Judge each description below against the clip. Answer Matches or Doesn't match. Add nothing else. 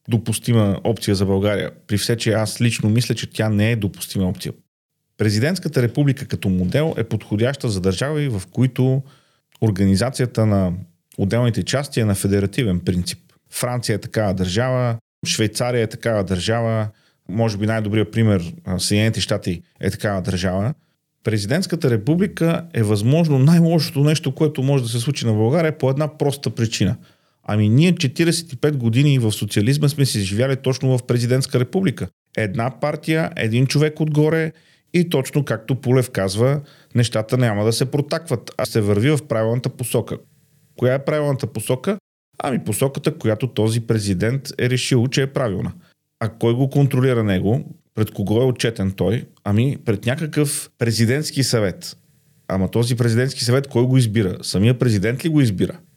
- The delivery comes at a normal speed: Matches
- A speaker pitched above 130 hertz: Doesn't match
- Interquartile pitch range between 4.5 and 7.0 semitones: Matches